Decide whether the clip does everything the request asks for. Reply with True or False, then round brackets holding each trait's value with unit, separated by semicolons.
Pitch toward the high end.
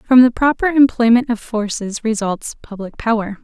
True (230 Hz)